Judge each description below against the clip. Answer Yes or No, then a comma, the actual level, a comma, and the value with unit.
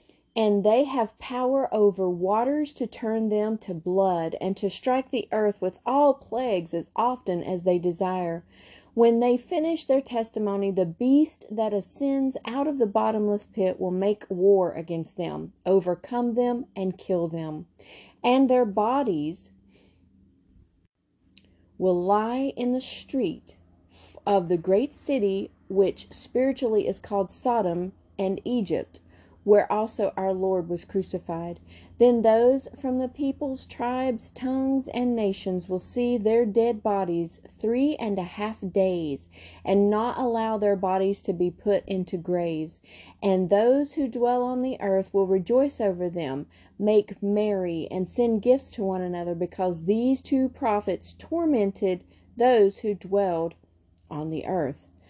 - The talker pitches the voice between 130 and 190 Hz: No, high, 200 Hz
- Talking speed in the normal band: Yes, average, 145 wpm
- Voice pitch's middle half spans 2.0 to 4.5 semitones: No, average, 5.1 semitones